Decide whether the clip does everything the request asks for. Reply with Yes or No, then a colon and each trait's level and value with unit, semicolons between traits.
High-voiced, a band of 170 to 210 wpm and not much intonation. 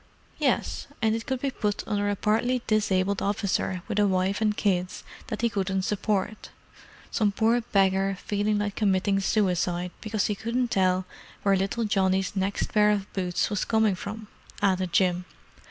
No: high, 200 Hz; average, 160 wpm; narrow, 2.2 semitones